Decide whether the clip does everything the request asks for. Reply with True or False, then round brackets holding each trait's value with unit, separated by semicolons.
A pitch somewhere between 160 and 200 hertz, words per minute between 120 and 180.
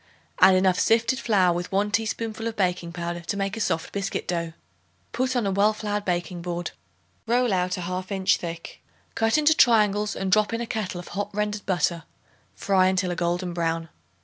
False (190 Hz; 195 wpm)